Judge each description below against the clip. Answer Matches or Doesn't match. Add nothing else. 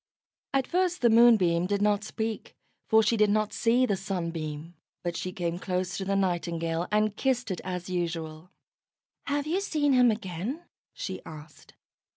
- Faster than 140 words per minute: Matches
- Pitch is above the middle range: Matches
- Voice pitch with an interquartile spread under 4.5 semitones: Doesn't match